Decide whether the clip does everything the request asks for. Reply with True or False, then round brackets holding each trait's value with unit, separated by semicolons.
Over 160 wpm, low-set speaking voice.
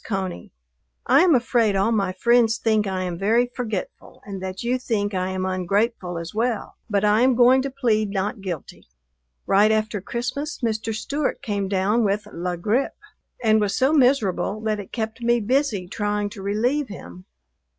False (175 wpm; 215 Hz)